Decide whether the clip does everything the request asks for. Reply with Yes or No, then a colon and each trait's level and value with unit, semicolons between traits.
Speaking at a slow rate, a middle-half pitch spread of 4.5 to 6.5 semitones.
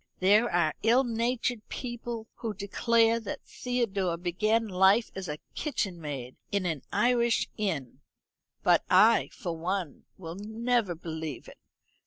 Yes: slow, 130 wpm; average, 5.1 semitones